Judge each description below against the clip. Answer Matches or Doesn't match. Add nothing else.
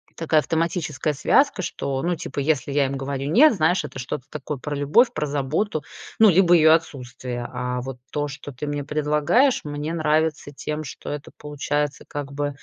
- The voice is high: Doesn't match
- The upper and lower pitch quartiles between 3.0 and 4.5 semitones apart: Doesn't match